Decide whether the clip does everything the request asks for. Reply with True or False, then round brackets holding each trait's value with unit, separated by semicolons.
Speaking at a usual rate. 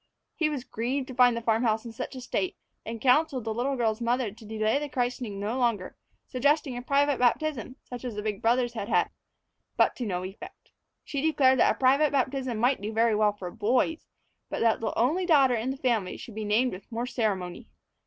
False (215 wpm)